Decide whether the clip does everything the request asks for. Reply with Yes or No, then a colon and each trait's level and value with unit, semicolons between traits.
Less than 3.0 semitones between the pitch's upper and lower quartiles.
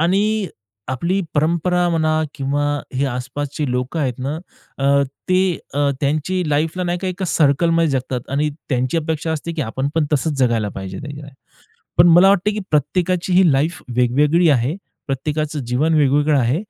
No: average, 3.9 semitones